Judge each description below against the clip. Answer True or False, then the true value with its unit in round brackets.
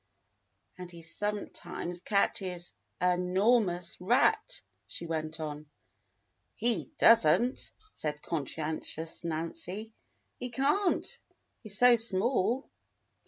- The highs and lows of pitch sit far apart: True (5.9 semitones)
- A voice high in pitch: False (180 Hz)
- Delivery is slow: True (100 wpm)